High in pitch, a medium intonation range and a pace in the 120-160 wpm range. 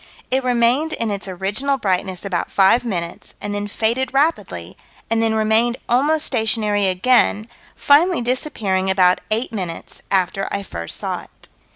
Yes: high, 220 Hz; average, 4.5 semitones; average, 150 wpm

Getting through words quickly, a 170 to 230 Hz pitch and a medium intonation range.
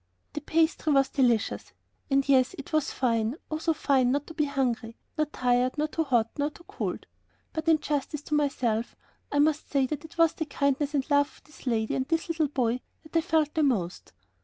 No: fast, 210 wpm; very high, 285 Hz; average, 3.4 semitones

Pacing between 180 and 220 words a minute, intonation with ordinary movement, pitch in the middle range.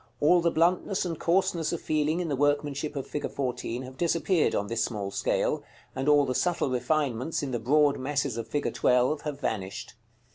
Yes: average, 190 wpm; average, 3.9 semitones; medium, 145 Hz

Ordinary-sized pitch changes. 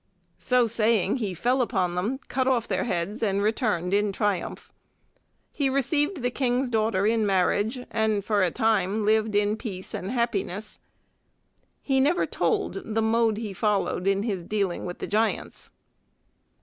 Yes: average, 3.3 semitones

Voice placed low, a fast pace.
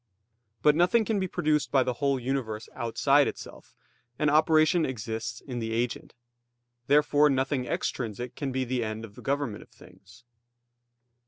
No: low, 130 Hz; average, 155 wpm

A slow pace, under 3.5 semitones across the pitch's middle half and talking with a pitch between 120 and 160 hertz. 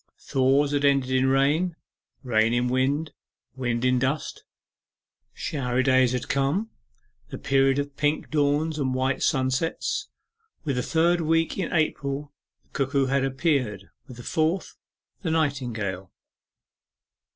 Yes: slow, 130 wpm; average, 2.9 semitones; low, 135 Hz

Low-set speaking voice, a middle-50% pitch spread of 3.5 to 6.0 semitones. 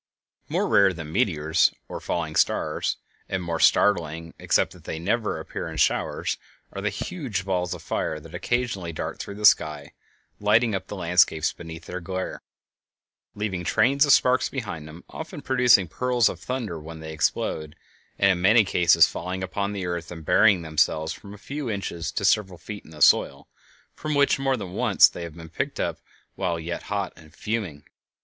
Yes: very low, 95 Hz; average, 4.4 semitones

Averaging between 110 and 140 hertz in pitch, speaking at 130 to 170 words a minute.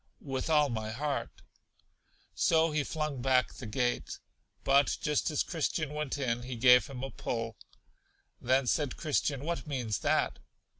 Yes: low, 135 Hz; average, 150 wpm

